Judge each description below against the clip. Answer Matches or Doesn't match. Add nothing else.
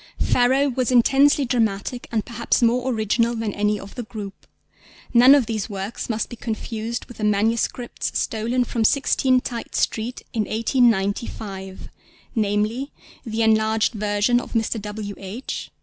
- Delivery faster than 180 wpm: Doesn't match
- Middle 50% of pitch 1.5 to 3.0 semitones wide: Matches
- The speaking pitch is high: Matches